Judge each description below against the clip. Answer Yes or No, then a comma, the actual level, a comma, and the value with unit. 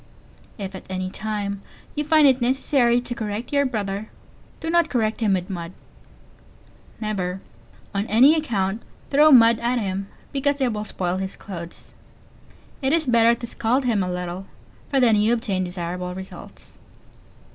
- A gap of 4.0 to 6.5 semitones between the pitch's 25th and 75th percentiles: Yes, average, 4.9 semitones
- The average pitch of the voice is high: Yes, high, 220 Hz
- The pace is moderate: Yes, average, 155 wpm